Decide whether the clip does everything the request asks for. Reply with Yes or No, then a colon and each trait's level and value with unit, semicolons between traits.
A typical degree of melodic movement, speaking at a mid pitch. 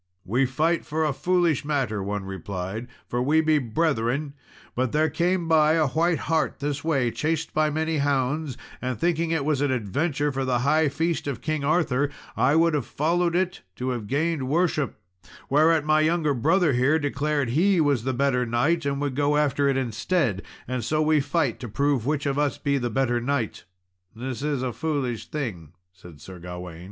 Yes: average, 3.9 semitones; medium, 145 Hz